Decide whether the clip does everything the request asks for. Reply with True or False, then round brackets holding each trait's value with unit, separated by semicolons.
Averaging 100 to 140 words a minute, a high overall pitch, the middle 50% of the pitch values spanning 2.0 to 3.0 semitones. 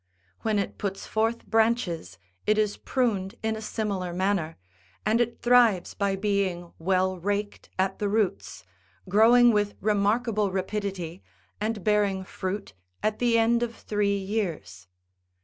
True (135 wpm; 205 Hz; 2.7 semitones)